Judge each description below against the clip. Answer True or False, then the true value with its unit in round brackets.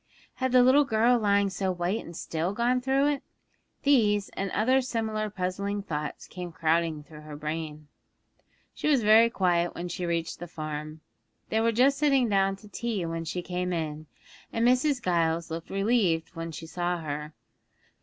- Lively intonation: True (5.7 semitones)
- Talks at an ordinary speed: True (175 wpm)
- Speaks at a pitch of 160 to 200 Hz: True (185 Hz)